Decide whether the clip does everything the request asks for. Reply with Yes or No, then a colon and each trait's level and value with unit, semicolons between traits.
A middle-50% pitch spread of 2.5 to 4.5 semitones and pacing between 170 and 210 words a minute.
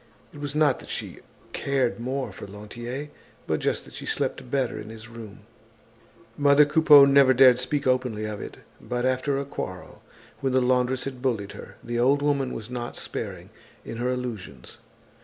Yes: average, 2.8 semitones; average, 175 wpm